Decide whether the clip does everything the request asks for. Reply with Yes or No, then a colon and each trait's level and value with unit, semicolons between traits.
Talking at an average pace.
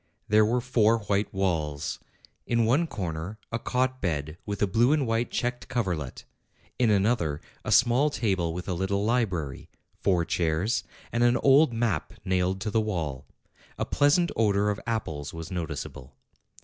Yes: average, 160 wpm